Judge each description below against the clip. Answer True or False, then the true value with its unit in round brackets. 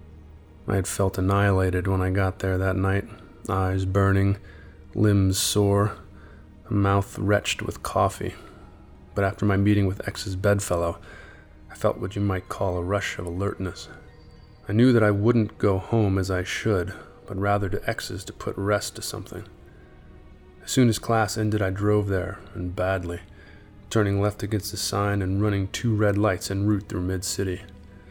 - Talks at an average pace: True (170 wpm)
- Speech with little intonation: True (1.9 semitones)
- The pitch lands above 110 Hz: False (100 Hz)